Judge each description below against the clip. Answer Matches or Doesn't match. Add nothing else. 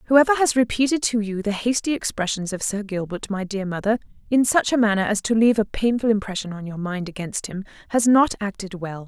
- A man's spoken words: Doesn't match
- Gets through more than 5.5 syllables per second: Matches